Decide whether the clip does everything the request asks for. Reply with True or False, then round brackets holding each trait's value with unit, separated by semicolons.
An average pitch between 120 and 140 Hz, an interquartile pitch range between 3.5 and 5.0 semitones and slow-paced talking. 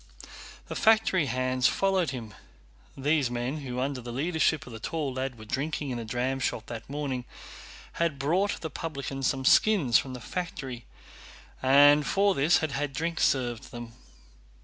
False (135 Hz; 4.0 semitones; 160 wpm)